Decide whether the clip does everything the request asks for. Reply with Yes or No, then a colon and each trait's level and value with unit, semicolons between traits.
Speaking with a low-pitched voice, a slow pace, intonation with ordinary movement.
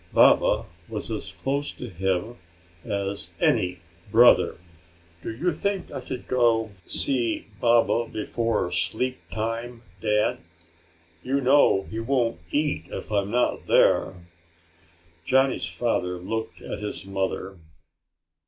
Yes: low, 115 Hz; slow, 115 wpm; average, 4.1 semitones